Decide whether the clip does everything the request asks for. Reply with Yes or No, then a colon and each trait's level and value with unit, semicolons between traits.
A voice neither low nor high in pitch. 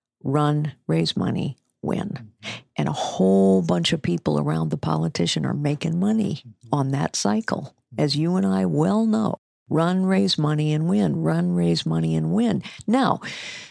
Yes: medium, 150 Hz